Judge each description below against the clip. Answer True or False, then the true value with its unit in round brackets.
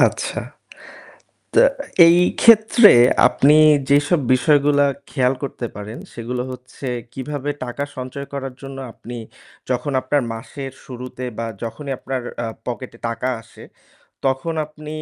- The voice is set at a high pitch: False (135 Hz)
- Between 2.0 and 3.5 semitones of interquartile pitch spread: True (2.5 semitones)